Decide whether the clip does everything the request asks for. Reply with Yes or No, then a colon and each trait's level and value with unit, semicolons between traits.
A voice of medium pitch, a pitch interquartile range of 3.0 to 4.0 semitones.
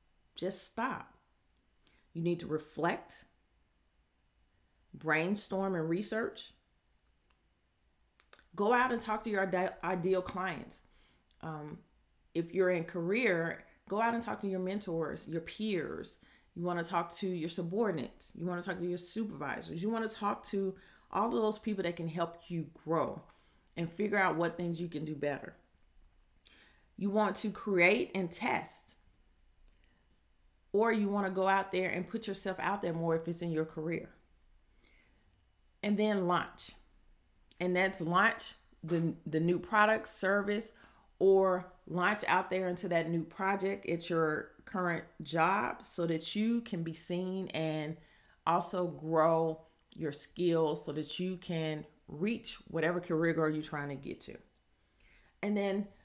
Yes: medium, 175 Hz; average, 3.6 semitones